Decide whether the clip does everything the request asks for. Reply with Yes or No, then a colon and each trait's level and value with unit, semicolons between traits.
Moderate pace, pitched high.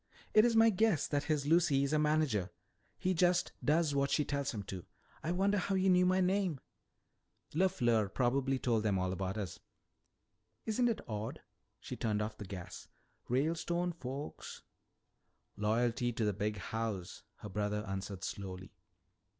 No: average, 160 wpm; low, 135 Hz